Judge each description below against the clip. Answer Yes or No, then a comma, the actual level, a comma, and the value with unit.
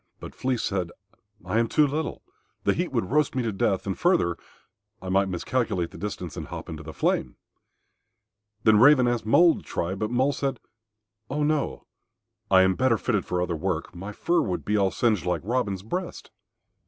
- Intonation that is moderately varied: No, wide, 5.9 semitones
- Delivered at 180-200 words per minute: Yes, average, 190 wpm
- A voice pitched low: Yes, low, 105 Hz